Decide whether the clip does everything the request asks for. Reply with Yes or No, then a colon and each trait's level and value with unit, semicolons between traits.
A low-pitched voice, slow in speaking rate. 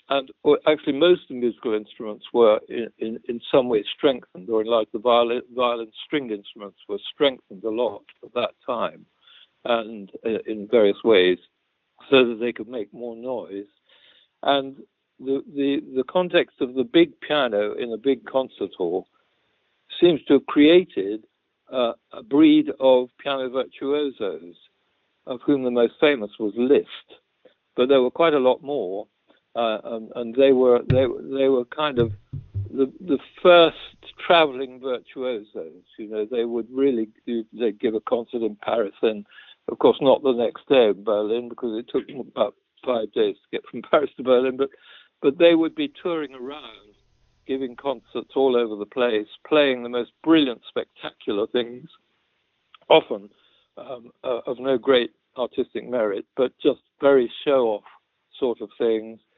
No: low, 130 Hz; average, 165 wpm